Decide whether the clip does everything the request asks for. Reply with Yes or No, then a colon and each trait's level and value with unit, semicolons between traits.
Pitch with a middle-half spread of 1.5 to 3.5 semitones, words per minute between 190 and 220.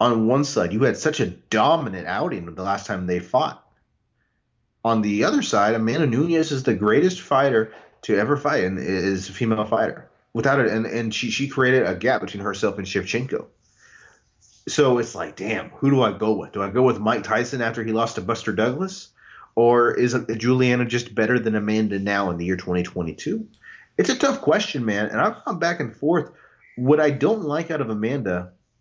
No: average, 4.1 semitones; average, 200 wpm